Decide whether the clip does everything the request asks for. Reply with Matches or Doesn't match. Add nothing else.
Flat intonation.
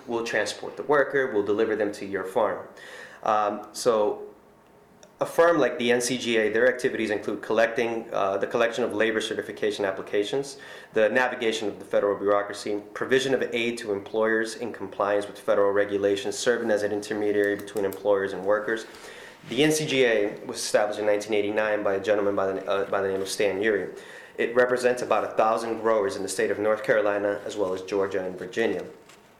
Doesn't match